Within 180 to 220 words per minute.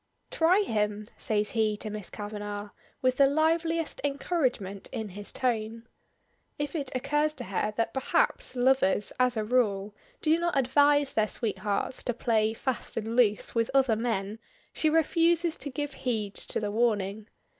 No: average, 155 wpm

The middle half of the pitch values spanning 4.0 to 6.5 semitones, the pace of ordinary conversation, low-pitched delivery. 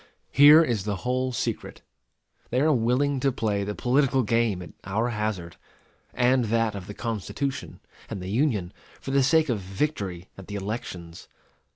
Yes: average, 4.7 semitones; average, 165 wpm; low, 115 Hz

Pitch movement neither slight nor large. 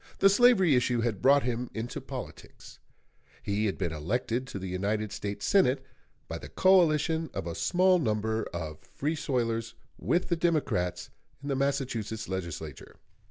No: wide, 6.9 semitones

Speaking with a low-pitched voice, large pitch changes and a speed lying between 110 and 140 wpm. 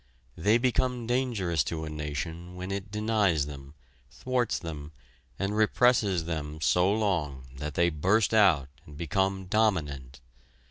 Yes: very low, 90 Hz; wide, 5.9 semitones; slow, 135 wpm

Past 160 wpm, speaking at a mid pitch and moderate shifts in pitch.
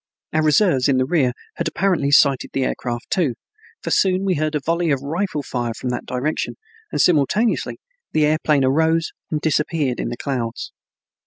Yes: average, 180 wpm; medium, 150 Hz; average, 4.0 semitones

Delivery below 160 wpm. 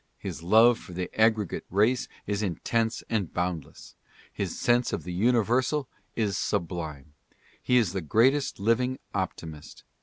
Yes: average, 140 wpm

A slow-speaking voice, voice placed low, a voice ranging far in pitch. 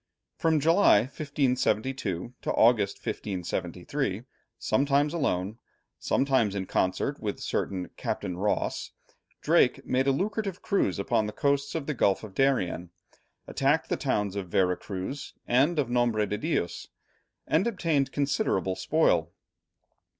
Yes: slow, 130 wpm; low, 125 Hz; wide, 6.4 semitones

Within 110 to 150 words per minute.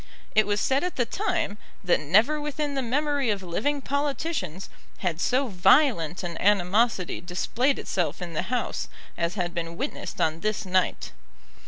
No: average, 160 wpm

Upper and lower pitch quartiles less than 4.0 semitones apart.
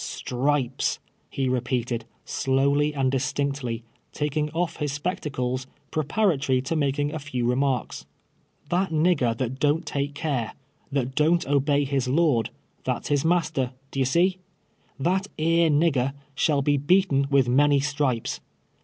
Yes: average, 2.8 semitones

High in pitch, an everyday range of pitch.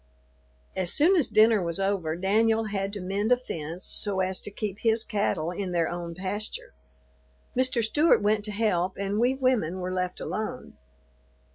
Yes: high, 200 Hz; average, 3.5 semitones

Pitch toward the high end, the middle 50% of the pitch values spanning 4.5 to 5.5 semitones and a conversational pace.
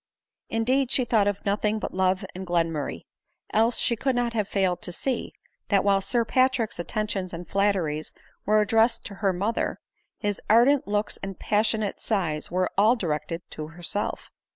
No: high, 205 Hz; average, 3.6 semitones; average, 165 wpm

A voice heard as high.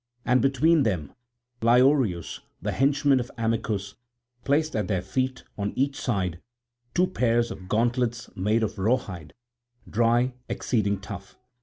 No: low, 115 Hz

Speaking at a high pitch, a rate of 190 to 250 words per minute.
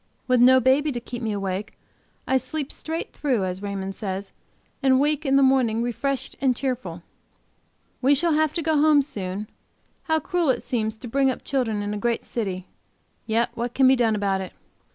Yes: high, 245 Hz; average, 195 wpm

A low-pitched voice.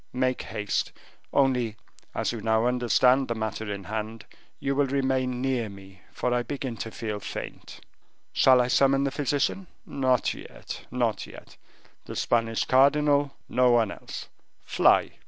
Yes: low, 125 Hz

